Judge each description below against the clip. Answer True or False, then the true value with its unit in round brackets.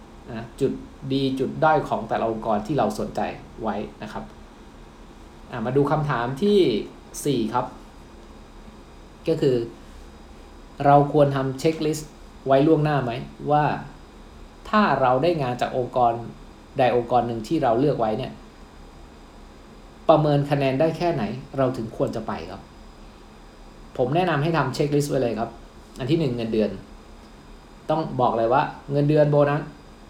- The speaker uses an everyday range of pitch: False (5.9 semitones)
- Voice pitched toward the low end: True (130 Hz)